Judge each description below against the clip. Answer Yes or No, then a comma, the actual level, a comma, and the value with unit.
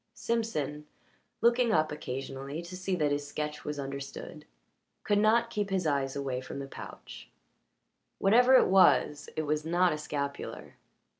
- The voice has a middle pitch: Yes, medium, 150 Hz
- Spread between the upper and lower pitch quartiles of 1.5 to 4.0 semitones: No, wide, 5.6 semitones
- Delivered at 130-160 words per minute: Yes, average, 150 wpm